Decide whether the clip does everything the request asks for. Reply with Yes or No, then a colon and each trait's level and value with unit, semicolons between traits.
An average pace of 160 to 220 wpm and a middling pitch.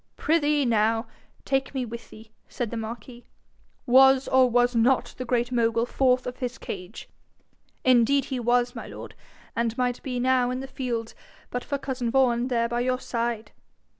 No: average, 170 wpm; high, 245 Hz